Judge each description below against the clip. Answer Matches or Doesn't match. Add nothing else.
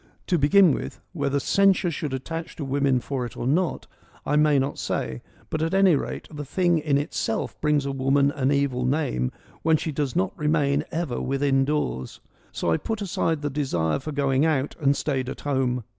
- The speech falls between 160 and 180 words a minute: Doesn't match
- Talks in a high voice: Doesn't match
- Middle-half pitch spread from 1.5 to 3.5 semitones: Matches